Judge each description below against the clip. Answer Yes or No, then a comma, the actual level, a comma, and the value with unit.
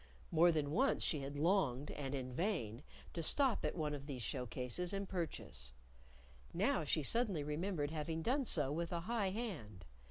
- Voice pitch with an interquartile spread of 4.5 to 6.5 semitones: Yes, wide, 5.4 semitones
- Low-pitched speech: No, medium, 160 Hz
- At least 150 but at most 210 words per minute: Yes, average, 180 wpm